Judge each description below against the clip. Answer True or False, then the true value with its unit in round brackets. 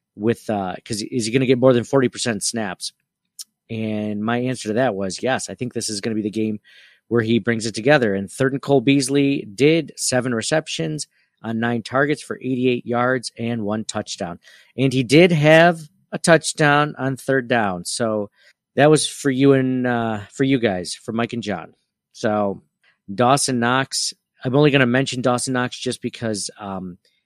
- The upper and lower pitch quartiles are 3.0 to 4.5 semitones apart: True (3.8 semitones)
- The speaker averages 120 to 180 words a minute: False (190 wpm)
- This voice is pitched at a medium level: False (125 Hz)